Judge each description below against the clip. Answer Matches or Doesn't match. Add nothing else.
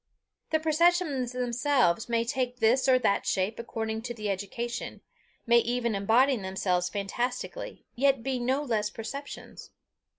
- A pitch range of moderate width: Matches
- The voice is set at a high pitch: Matches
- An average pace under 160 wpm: Matches